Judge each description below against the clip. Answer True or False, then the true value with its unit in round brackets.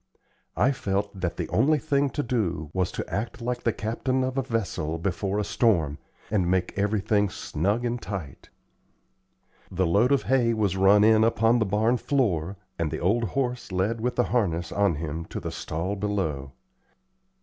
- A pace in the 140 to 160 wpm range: False (175 wpm)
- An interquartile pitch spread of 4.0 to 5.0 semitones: True (4.7 semitones)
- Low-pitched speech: True (105 Hz)